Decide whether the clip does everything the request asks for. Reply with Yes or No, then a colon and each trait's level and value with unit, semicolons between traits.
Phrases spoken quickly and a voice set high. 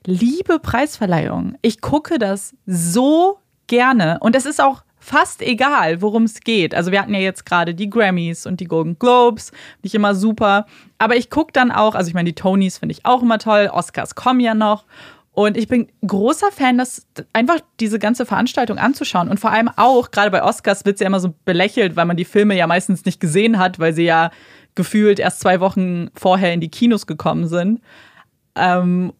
Yes: fast, 200 wpm; high, 210 Hz